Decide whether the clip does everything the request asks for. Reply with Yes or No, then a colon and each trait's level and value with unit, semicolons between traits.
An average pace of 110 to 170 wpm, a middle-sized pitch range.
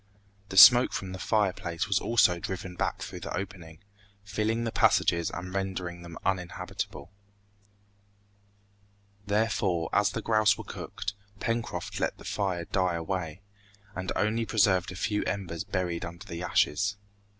Yes: average, 140 wpm; average, 3.0 semitones